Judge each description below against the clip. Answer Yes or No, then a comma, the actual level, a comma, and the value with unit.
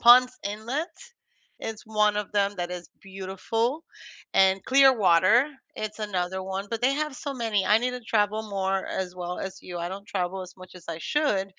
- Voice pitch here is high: Yes, high, 205 Hz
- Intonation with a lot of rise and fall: No, average, 3.7 semitones